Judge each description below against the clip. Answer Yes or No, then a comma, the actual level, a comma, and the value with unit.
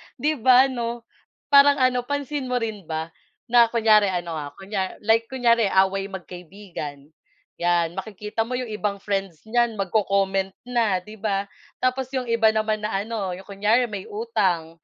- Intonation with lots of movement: No, average, 3.7 semitones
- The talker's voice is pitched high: Yes, high, 210 Hz